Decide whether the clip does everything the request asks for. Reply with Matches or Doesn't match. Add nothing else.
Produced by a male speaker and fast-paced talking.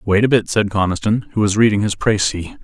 Matches